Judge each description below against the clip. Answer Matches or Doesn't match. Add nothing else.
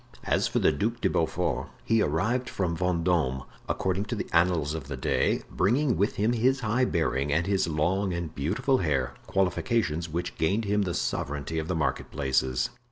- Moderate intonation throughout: Matches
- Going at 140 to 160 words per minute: Doesn't match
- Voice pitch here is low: Matches